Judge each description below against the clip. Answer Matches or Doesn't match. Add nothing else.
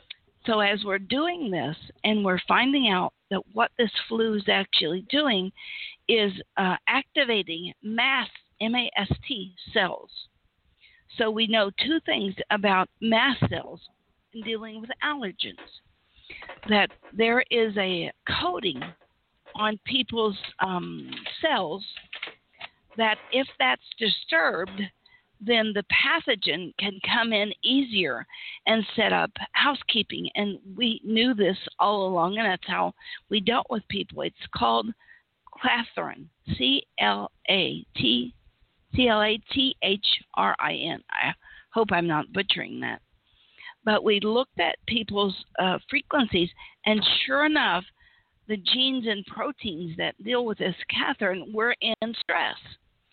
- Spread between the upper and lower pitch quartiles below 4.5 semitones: Matches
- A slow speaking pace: Matches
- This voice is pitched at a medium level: Doesn't match